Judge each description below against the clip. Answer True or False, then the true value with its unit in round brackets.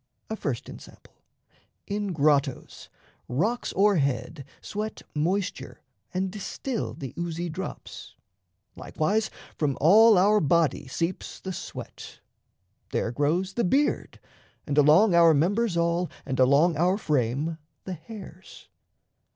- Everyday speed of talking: False (115 wpm)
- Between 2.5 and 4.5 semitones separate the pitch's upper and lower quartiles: False (5.1 semitones)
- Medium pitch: True (170 Hz)